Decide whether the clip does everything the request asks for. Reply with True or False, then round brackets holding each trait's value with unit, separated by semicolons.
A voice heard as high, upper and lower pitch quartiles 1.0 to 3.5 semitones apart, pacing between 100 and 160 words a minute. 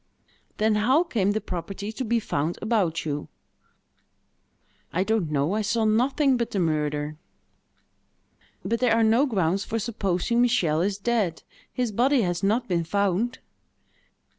False (210 Hz; 5.1 semitones; 145 wpm)